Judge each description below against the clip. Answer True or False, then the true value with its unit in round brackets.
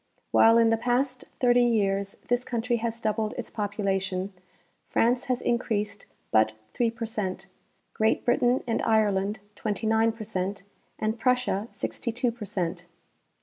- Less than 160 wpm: True (140 wpm)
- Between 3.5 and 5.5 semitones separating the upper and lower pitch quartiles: False (3.0 semitones)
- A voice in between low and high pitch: False (220 Hz)